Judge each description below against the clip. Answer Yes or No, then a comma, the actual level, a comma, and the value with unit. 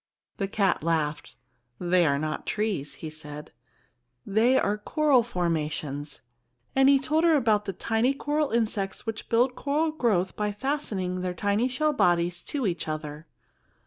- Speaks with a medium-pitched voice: No, high, 205 Hz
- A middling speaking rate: Yes, average, 150 wpm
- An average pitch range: No, wide, 7.3 semitones